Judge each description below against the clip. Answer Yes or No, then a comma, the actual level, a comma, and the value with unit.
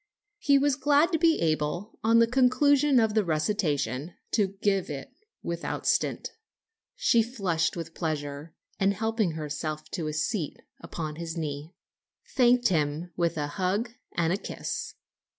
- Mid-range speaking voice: Yes, medium, 180 Hz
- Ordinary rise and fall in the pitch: No, wide, 6.8 semitones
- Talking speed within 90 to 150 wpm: Yes, average, 145 wpm